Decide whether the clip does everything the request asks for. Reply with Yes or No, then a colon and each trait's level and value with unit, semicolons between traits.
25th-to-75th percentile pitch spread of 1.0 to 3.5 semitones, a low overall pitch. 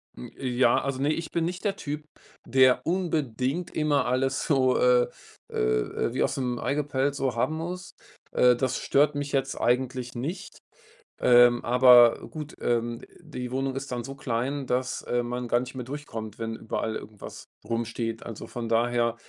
Yes: average, 2.9 semitones; low, 130 Hz